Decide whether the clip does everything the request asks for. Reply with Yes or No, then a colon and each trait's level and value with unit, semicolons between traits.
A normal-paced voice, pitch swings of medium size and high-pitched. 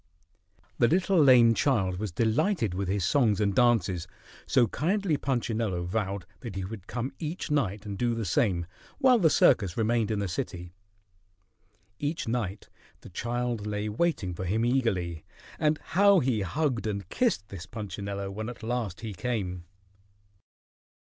No: average, 155 wpm; average, 4.3 semitones; low, 110 Hz